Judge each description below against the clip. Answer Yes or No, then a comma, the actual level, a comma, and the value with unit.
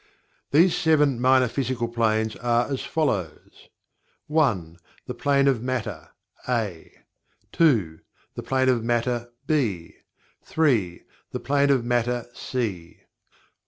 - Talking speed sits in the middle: No, slow, 120 wpm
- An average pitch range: Yes, average, 3.9 semitones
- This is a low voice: Yes, low, 120 Hz